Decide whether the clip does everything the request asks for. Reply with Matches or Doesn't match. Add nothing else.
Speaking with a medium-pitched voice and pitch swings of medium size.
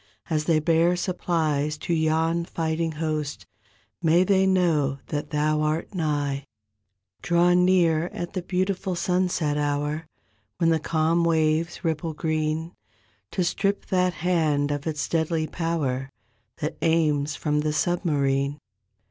Doesn't match